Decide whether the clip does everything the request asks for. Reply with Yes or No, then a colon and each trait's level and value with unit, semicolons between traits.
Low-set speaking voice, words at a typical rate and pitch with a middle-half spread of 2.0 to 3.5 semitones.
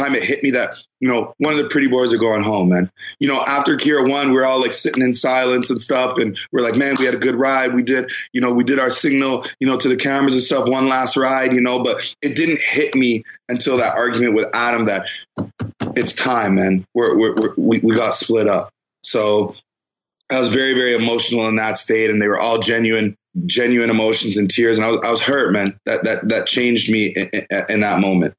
No: low, 125 Hz; fast, 240 wpm; average, 2.9 semitones